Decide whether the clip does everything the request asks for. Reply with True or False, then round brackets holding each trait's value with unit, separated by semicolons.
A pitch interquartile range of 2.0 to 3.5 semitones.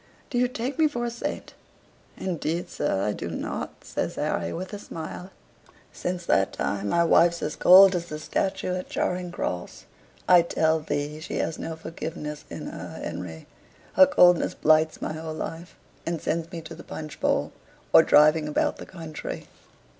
True (2.8 semitones)